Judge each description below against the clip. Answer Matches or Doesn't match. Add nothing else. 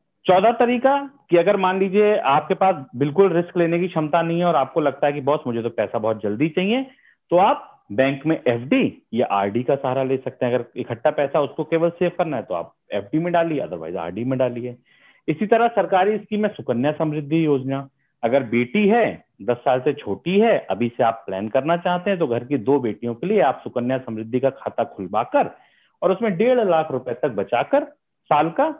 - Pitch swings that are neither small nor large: Doesn't match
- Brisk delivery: Matches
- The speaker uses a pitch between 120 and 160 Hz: Matches